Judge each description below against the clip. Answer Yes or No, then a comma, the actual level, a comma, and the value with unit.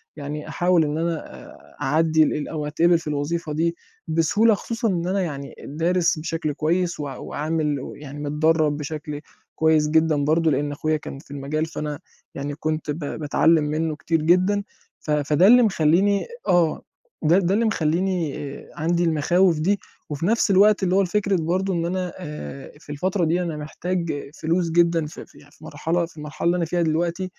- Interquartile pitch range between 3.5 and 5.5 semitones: No, average, 2.7 semitones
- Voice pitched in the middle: Yes, medium, 160 Hz